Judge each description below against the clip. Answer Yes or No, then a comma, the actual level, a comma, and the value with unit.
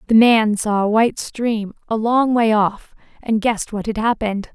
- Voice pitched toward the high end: Yes, high, 220 Hz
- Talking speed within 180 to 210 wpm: Yes, average, 200 wpm